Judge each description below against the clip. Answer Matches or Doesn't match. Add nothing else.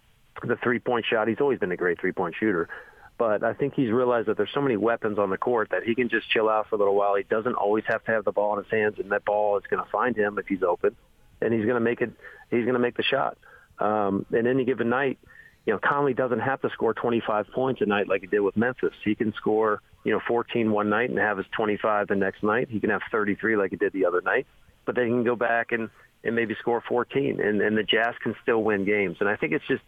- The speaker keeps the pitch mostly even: Matches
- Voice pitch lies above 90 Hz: Matches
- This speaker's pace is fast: Matches